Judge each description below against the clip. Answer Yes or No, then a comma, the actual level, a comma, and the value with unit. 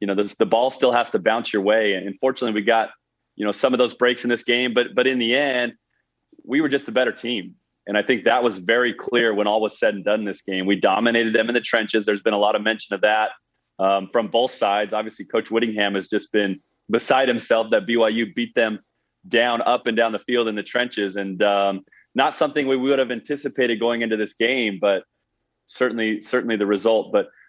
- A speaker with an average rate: No, fast, 235 wpm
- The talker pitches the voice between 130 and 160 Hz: No, low, 115 Hz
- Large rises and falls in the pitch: No, average, 2.8 semitones